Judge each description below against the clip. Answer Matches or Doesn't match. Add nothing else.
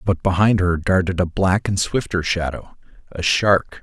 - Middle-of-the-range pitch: Doesn't match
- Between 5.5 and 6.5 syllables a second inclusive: Doesn't match